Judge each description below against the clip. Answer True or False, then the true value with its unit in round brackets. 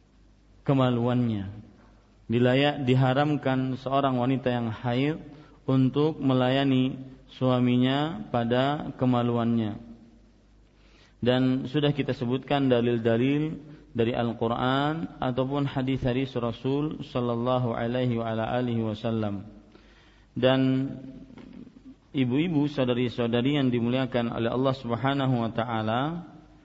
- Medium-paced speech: False (80 wpm)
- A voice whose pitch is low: True (125 Hz)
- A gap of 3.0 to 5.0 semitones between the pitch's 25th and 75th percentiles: False (2.6 semitones)